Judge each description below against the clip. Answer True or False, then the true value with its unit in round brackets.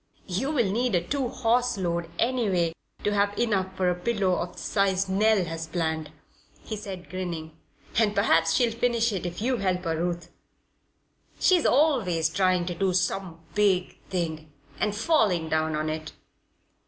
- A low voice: False (190 Hz)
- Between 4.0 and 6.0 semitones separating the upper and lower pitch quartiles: True (4.4 semitones)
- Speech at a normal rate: True (160 wpm)